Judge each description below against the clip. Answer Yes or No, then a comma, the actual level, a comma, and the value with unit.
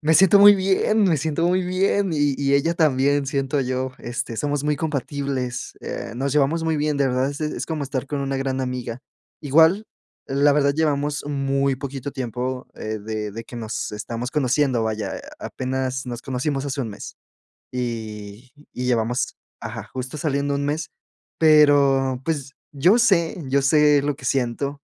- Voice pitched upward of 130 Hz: Yes, medium, 140 Hz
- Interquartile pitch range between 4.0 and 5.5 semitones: No, average, 2.8 semitones